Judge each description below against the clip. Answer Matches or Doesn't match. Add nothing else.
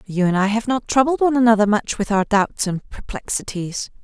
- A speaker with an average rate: Doesn't match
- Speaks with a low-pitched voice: Doesn't match